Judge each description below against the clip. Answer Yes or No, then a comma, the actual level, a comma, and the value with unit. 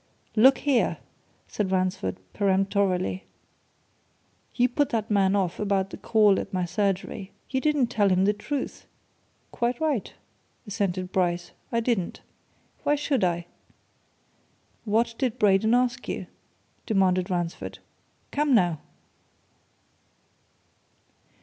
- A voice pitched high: Yes, high, 200 Hz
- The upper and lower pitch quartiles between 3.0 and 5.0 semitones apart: Yes, average, 4.4 semitones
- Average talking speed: No, slow, 110 wpm